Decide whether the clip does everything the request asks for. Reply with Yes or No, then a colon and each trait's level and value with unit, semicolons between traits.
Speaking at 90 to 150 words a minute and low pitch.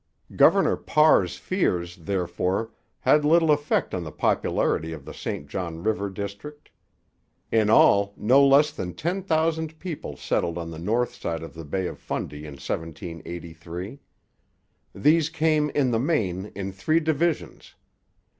Yes: average, 145 wpm; low, 100 Hz